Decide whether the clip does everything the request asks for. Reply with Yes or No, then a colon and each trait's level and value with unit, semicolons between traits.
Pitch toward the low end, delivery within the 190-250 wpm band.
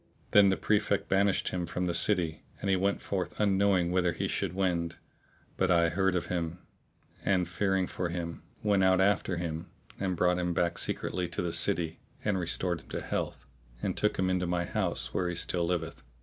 Yes: very low, 90 Hz; average, 195 wpm